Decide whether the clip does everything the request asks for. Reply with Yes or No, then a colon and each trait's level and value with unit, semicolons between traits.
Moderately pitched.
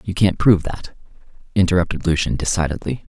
No: very low, 90 Hz